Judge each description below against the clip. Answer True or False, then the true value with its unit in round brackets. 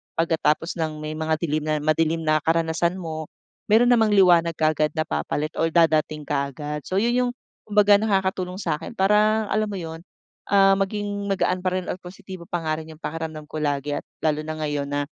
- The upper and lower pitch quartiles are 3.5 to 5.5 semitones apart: True (4.0 semitones)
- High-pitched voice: False (165 Hz)